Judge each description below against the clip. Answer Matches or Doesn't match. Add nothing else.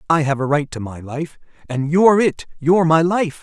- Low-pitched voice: Doesn't match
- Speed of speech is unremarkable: Doesn't match